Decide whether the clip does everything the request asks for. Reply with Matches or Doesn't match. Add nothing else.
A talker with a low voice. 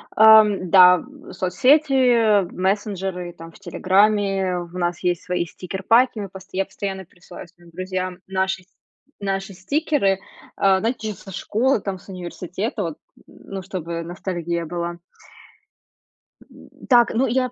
Doesn't match